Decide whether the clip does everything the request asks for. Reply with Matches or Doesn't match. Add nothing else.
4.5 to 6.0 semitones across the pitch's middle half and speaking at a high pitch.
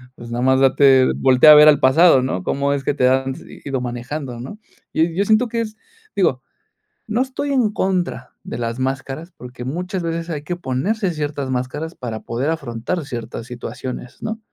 Doesn't match